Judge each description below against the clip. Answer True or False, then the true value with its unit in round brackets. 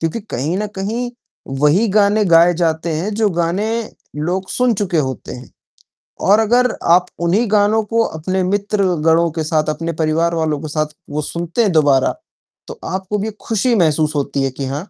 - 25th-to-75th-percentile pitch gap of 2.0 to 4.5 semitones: False (4.9 semitones)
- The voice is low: False (175 Hz)